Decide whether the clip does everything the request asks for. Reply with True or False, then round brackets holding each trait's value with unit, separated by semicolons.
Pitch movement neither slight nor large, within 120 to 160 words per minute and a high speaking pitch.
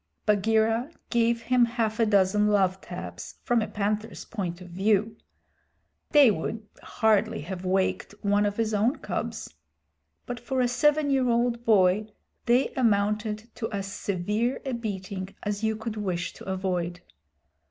True (3.2 semitones; 150 wpm; 215 Hz)